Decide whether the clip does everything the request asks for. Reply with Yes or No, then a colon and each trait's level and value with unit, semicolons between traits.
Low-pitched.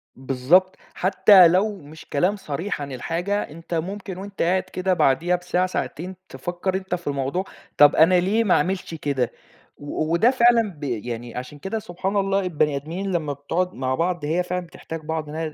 No: medium, 175 Hz